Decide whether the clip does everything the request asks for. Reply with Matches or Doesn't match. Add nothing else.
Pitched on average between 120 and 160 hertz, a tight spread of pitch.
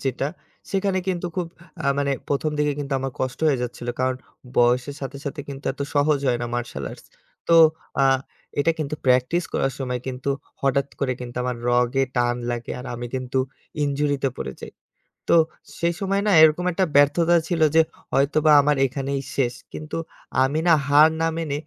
Doesn't match